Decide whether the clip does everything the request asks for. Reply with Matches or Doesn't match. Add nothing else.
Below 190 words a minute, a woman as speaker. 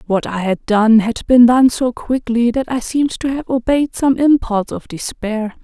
Doesn't match